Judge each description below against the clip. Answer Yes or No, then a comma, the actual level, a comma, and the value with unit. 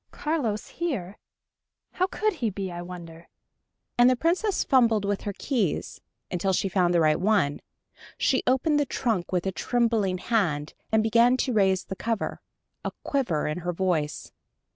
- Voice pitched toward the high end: Yes, high, 205 Hz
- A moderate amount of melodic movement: No, wide, 5.8 semitones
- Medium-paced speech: Yes, average, 165 wpm